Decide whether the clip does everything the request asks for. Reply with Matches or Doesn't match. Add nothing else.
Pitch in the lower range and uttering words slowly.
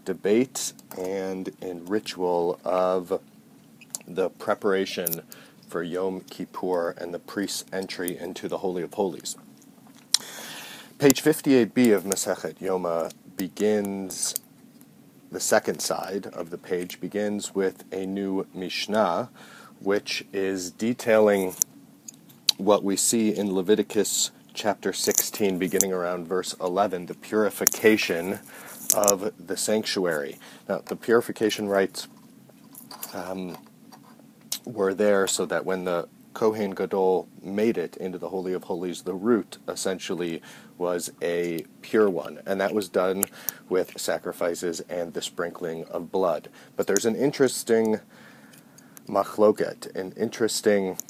Matches